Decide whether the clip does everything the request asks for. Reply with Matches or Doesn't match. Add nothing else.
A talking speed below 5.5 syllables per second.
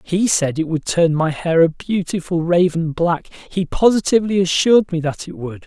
Matches